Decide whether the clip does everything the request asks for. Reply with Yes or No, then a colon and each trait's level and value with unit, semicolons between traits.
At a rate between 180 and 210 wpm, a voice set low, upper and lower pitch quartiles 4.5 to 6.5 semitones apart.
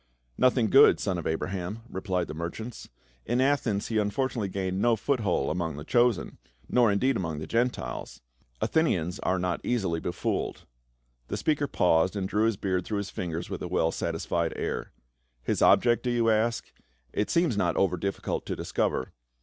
Yes: average, 185 wpm; low, 100 Hz; wide, 5.4 semitones